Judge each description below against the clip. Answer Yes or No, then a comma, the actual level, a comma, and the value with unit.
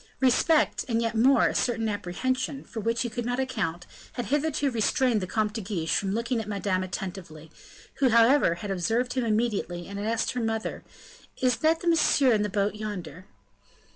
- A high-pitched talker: Yes, high, 225 Hz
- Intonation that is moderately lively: Yes, average, 4.0 semitones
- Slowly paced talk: No, average, 190 wpm